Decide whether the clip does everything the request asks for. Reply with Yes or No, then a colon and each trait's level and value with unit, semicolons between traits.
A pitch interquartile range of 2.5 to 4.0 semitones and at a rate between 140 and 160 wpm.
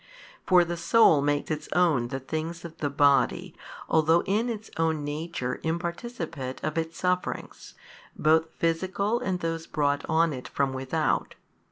Yes: average, 3.0 semitones; average, 150 wpm